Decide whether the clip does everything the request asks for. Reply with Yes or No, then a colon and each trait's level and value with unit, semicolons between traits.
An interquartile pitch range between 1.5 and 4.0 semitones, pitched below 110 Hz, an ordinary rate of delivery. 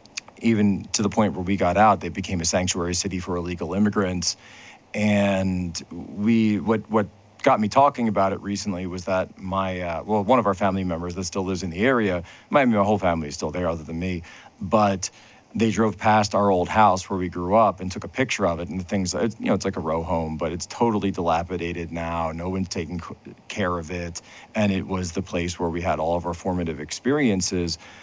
No: average, 2.9 semitones; very low, 95 Hz; fast, 220 wpm